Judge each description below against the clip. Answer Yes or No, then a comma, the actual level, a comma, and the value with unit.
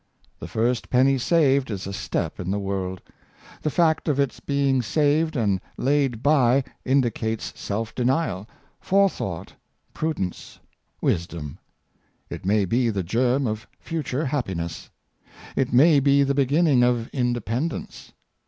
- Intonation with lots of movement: No, average, 4.8 semitones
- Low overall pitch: Yes, low, 125 Hz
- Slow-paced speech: Yes, slow, 130 wpm